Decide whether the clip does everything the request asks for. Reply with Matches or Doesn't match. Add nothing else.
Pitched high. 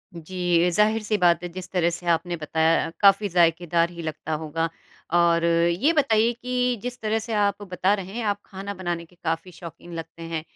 Doesn't match